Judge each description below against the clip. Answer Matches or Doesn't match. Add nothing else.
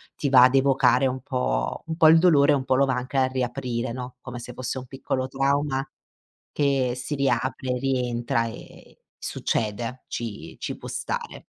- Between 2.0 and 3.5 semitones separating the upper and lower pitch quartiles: Doesn't match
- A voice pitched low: Matches